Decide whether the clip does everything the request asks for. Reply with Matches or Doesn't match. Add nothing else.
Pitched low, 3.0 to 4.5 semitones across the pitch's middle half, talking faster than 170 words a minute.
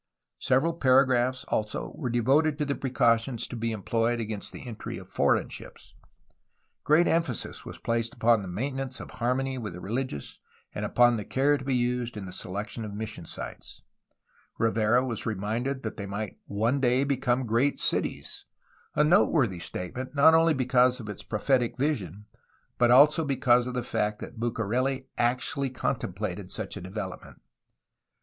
Doesn't match